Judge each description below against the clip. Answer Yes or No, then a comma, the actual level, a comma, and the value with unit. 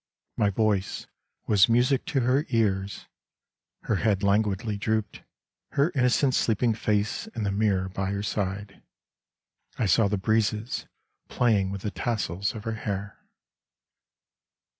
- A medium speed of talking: No, slow, 130 wpm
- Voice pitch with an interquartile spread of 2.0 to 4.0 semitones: Yes, narrow, 2.5 semitones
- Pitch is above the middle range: No, low, 105 Hz